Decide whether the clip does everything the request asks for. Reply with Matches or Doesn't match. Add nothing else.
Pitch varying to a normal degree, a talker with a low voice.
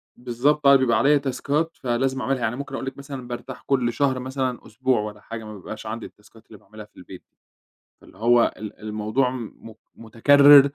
Matches